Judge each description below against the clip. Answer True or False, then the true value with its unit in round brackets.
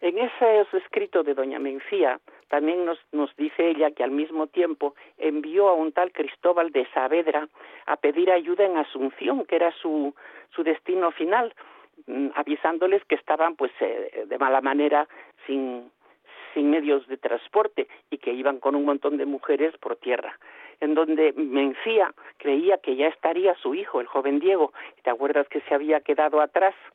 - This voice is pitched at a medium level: True (155 Hz)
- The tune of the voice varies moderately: True (4.7 semitones)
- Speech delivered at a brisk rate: False (165 wpm)